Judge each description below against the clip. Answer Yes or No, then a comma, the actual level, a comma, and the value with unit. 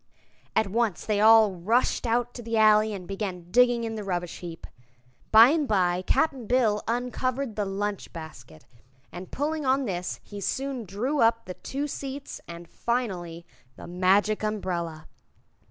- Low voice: No, high, 215 Hz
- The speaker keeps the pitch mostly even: No, average, 5.0 semitones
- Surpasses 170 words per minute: No, average, 155 wpm